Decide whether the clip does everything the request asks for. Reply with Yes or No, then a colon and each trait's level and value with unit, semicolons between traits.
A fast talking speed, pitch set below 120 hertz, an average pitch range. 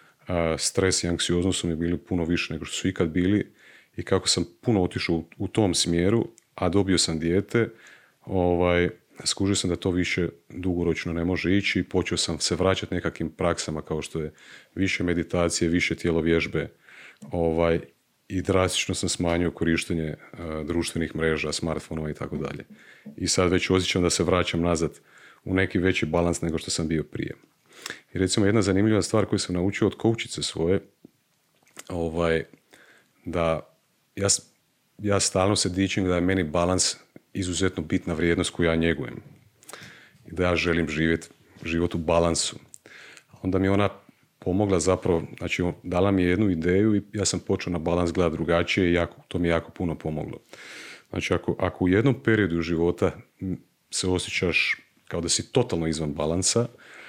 No: fast, 165 wpm; very low, 90 Hz; narrow, 2.2 semitones